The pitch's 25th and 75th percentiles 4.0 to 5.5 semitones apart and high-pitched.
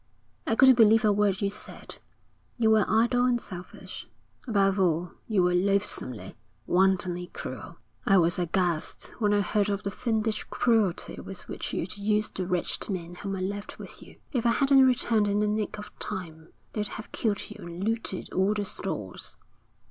No: average, 3.0 semitones; high, 205 Hz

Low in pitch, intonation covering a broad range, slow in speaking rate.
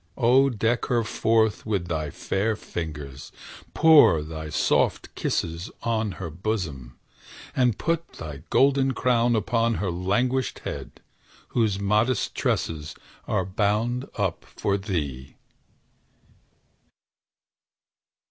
Yes: low, 105 Hz; wide, 6.1 semitones; slow, 105 wpm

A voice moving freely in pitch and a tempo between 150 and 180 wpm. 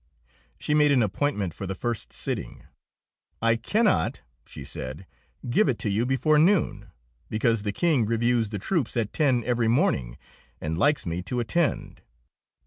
Yes: wide, 5.9 semitones; average, 155 wpm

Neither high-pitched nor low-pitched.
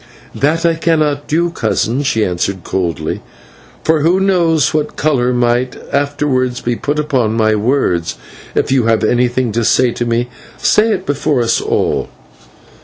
No: low, 130 Hz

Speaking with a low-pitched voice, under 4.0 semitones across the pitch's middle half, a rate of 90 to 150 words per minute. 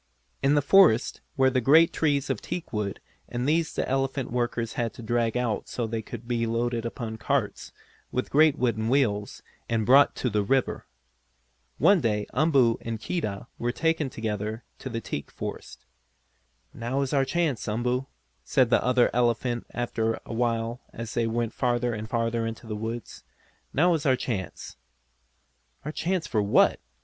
No: low, 120 Hz; average, 3.0 semitones; average, 165 wpm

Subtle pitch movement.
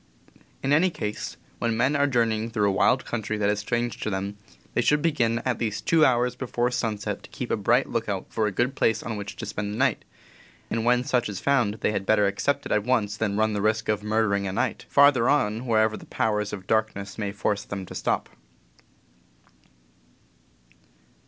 No: average, 3.0 semitones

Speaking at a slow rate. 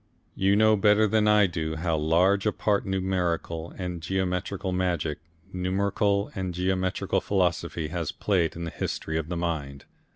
No: average, 155 wpm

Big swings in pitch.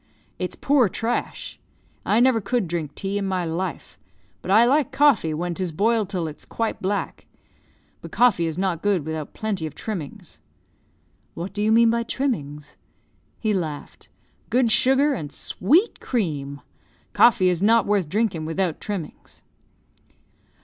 Yes: wide, 5.8 semitones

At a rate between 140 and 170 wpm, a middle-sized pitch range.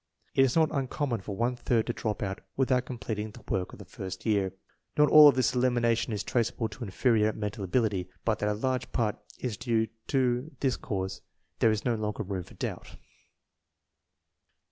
No: average, 190 wpm; average, 3.3 semitones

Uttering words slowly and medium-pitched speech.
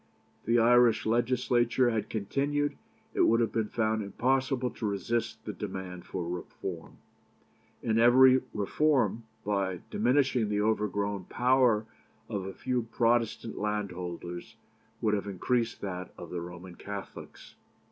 No: slow, 130 wpm; low, 110 Hz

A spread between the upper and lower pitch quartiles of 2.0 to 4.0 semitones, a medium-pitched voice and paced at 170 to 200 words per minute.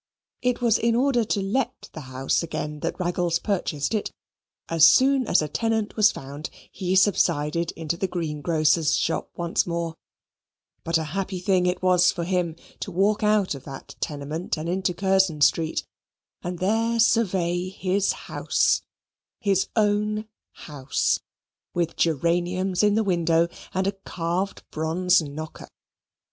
No: average, 3.5 semitones; medium, 180 Hz; average, 145 wpm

